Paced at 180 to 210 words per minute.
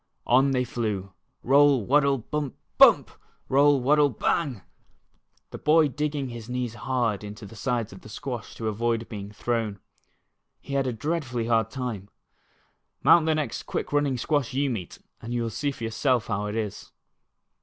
No: average, 170 wpm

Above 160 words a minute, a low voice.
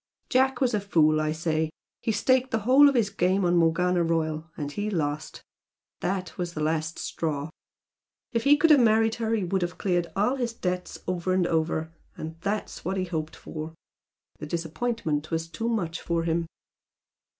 No: average, 185 wpm; medium, 175 Hz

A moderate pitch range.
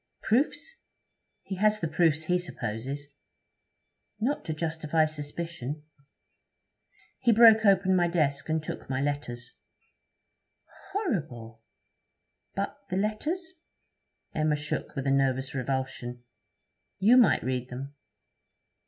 No: wide, 6.4 semitones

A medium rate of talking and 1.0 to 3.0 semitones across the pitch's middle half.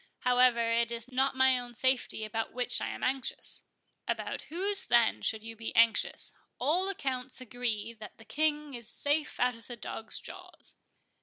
Yes: average, 165 wpm; narrow, 2.6 semitones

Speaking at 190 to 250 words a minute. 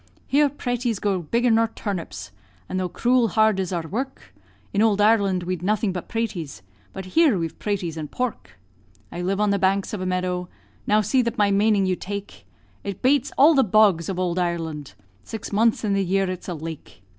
Yes: average, 200 wpm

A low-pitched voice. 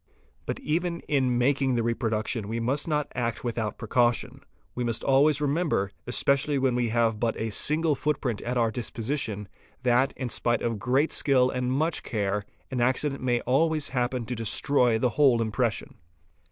Yes: low, 125 Hz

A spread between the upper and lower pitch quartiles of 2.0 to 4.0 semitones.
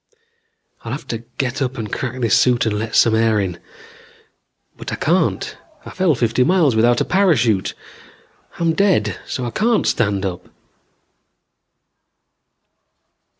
No: average, 4.8 semitones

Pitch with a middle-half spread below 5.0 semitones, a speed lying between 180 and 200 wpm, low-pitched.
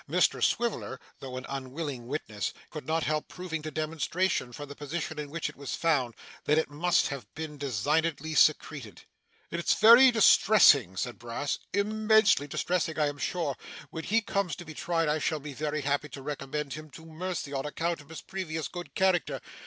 No: average, 3.3 semitones; average, 185 wpm; medium, 155 Hz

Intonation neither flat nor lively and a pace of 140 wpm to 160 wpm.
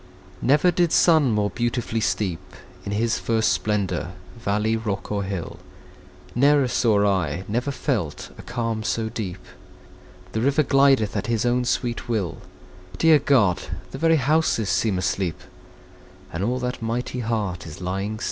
Yes: average, 4.0 semitones; average, 150 wpm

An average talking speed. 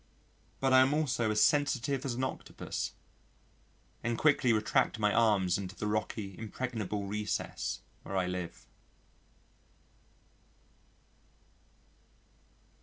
No: slow, 105 wpm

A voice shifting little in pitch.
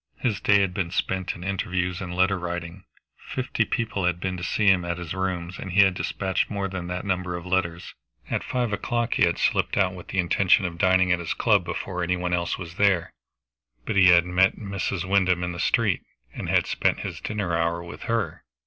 Yes: narrow, 1.9 semitones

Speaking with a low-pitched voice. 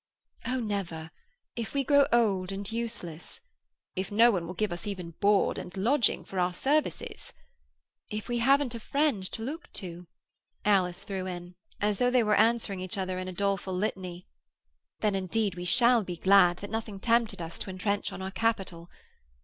No: high, 200 Hz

